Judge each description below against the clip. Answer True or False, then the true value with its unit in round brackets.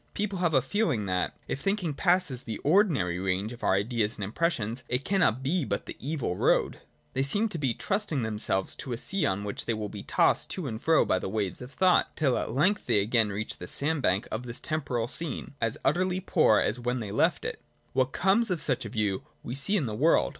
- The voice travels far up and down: True (7.5 semitones)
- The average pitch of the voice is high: False (130 Hz)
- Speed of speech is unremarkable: False (230 wpm)